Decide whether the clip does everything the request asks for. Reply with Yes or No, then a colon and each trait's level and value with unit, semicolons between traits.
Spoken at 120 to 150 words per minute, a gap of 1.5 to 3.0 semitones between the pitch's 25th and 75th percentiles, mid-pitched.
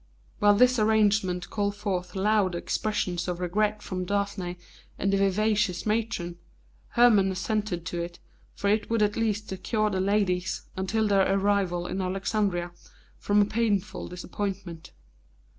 No: average, 140 wpm; narrow, 2.6 semitones; high, 200 Hz